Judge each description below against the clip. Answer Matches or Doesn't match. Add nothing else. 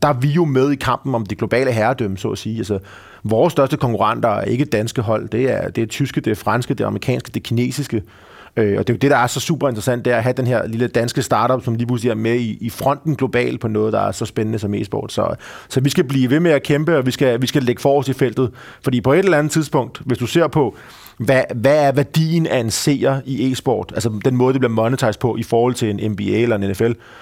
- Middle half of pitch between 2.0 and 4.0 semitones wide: Matches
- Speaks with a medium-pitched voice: Doesn't match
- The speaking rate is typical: Doesn't match